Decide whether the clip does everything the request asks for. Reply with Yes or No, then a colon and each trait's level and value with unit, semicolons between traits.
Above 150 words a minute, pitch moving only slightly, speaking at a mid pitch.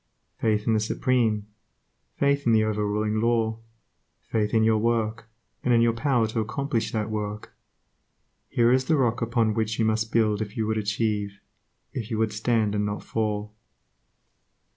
No: average, 170 wpm; narrow, 1.5 semitones; low, 110 Hz